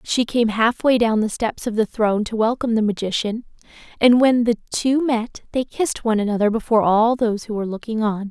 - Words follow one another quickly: Yes, fast, 210 wpm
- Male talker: No, female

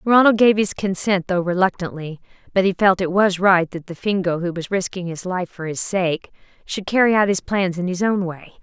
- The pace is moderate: No, fast, 225 wpm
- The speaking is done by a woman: Yes, female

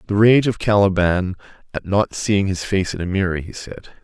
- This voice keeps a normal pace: No, fast, 210 wpm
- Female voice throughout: No, male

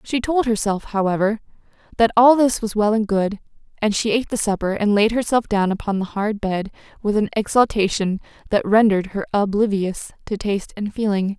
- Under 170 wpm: No, average, 185 wpm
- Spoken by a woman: Yes, female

